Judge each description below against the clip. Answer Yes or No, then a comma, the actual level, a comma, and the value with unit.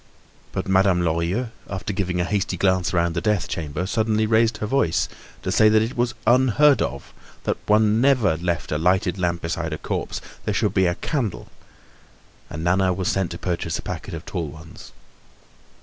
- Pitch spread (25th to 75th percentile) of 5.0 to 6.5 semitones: No, average, 4.1 semitones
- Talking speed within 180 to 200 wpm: Yes, average, 185 wpm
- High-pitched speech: No, very low, 95 Hz